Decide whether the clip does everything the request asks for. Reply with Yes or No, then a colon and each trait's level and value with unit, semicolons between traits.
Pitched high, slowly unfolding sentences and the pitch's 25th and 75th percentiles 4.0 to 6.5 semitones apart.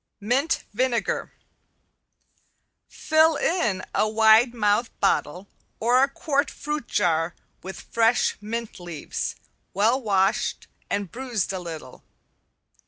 Yes: high, 225 Hz; slow, 105 wpm; average, 4.9 semitones